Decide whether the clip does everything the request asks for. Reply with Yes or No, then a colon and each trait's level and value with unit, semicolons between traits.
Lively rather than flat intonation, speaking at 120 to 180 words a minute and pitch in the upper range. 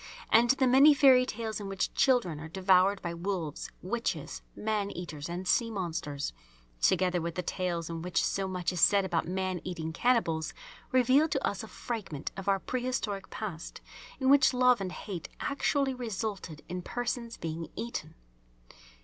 Yes: wide, 5.7 semitones; average, 165 wpm; high, 195 Hz